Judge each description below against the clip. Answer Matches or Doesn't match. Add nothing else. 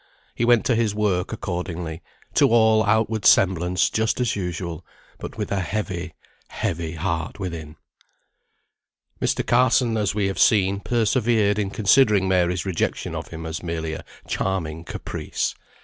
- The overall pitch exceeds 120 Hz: Doesn't match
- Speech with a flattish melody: Doesn't match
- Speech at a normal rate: Matches